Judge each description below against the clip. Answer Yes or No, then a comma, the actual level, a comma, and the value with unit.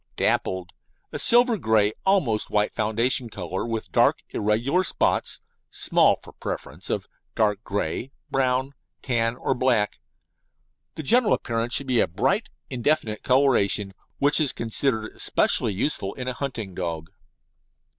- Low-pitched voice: Yes, low, 115 Hz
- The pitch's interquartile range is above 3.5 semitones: Yes, average, 4.5 semitones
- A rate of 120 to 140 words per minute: Yes, slow, 135 wpm